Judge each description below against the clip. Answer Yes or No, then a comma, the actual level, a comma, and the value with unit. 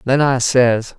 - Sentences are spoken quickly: No, average, 185 wpm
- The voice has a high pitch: No, low, 125 Hz